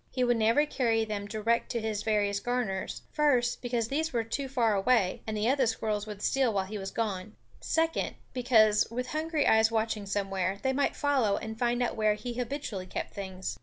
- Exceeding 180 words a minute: Yes, average, 200 wpm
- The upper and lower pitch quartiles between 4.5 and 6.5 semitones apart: No, average, 3.2 semitones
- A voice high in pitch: Yes, high, 225 Hz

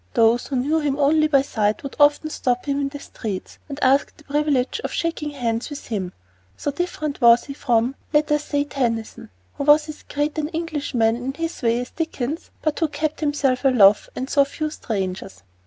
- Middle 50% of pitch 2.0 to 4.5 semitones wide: Yes, average, 3.7 semitones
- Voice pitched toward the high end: Yes, very high, 280 Hz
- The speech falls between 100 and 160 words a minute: No, average, 200 wpm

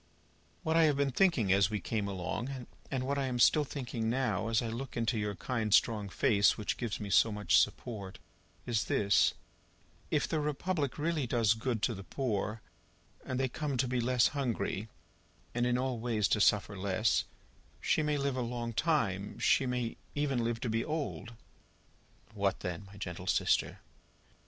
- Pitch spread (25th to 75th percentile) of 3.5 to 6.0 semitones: Yes, average, 4.1 semitones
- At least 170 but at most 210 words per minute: Yes, average, 180 wpm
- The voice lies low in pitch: Yes, low, 120 Hz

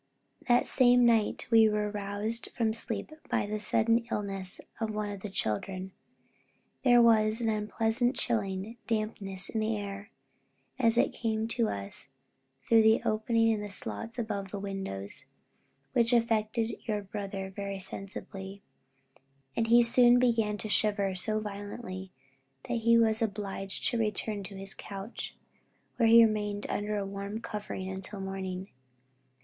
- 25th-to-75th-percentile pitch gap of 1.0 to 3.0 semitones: Yes, narrow, 2.4 semitones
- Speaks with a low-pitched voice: No, high, 210 Hz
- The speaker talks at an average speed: Yes, average, 145 wpm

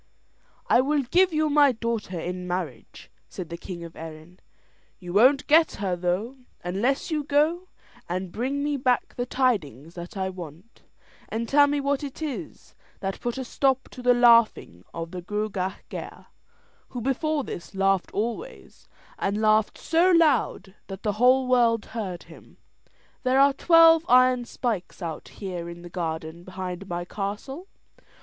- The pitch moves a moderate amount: No, wide, 6.9 semitones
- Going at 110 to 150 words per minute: No, average, 160 wpm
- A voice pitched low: No, high, 220 Hz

